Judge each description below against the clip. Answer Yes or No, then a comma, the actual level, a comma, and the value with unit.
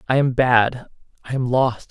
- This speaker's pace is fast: No, average, 190 wpm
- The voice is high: No, low, 125 Hz